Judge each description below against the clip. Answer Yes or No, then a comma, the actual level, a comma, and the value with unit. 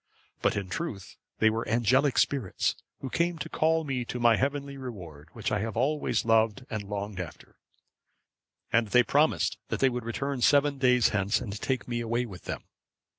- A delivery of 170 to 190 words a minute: Yes, average, 180 wpm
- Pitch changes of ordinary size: Yes, average, 4.3 semitones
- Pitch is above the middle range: No, low, 120 Hz